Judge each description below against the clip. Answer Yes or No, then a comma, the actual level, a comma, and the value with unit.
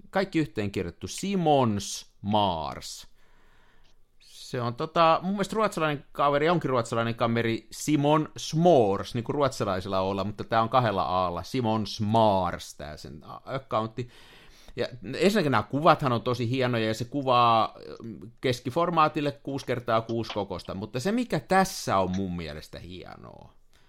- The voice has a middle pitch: No, low, 120 Hz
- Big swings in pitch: Yes, wide, 6.2 semitones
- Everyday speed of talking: Yes, average, 135 wpm